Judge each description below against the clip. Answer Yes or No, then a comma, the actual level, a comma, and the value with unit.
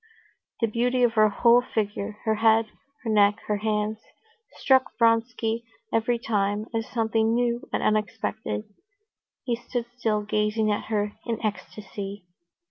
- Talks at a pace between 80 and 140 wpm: Yes, slow, 135 wpm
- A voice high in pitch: Yes, high, 220 Hz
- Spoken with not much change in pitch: Yes, narrow, 1.7 semitones